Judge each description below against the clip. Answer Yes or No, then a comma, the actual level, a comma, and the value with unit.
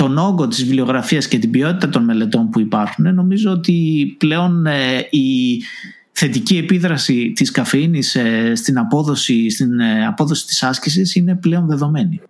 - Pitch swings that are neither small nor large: No, wide, 5.7 semitones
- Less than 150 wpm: Yes, average, 135 wpm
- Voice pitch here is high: No, medium, 155 Hz